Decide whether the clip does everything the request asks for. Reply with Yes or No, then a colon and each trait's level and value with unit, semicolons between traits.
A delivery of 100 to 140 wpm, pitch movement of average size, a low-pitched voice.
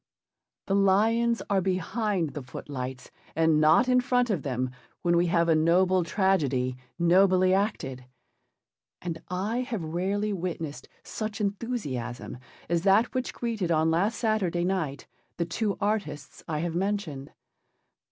No: slow, 135 wpm; average, 4.6 semitones; medium, 180 Hz